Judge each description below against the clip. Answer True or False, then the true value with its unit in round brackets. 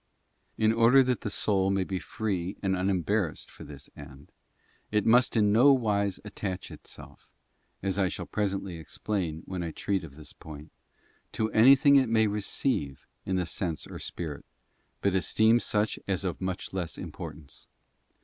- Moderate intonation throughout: True (4.0 semitones)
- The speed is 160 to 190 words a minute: True (175 wpm)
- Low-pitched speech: True (95 Hz)